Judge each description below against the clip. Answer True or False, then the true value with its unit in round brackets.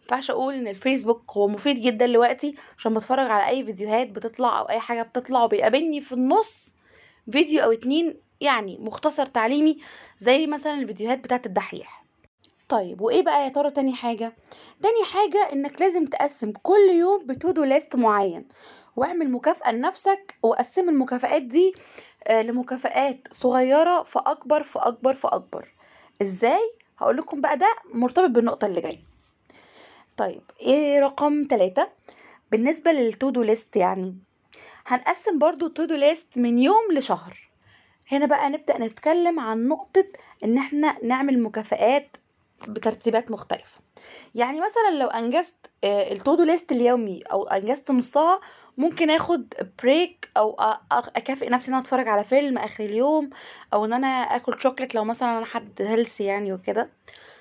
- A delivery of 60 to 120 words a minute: False (135 wpm)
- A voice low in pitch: False (265 Hz)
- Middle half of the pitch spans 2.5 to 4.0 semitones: False (5.1 semitones)